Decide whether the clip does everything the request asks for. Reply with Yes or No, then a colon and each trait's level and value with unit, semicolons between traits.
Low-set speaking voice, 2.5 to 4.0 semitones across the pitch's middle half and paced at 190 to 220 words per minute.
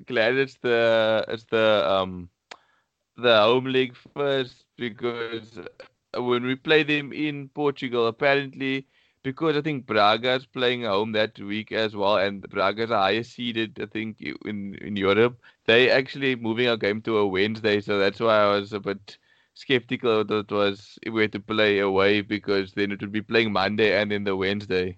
No: low, 110 Hz; average, 3.6 semitones; average, 180 wpm